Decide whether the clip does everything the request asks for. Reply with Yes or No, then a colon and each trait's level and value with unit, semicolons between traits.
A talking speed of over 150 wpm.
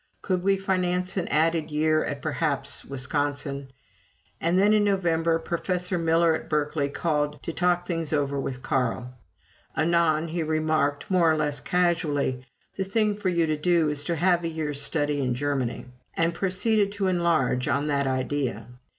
Yes: average, 165 wpm